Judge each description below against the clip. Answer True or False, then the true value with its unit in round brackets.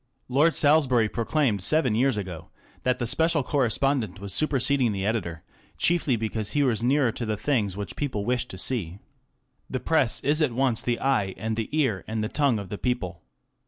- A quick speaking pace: False (195 wpm)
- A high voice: False (120 Hz)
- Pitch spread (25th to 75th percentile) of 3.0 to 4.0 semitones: False (4.7 semitones)